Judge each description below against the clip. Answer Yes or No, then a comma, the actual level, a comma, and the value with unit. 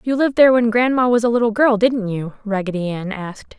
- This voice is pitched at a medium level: No, high, 225 Hz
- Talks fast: Yes, fast, 235 wpm